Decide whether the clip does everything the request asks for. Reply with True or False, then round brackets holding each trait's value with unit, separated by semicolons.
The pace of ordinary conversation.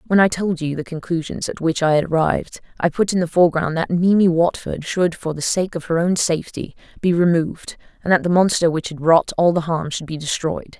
False (230 wpm)